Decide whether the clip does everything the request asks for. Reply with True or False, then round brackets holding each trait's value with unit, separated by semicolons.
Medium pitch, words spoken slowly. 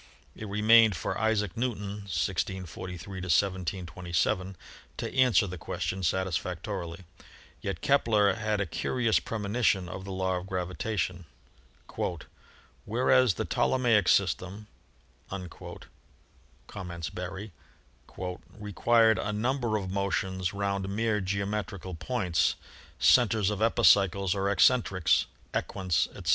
False (100 Hz; 105 wpm)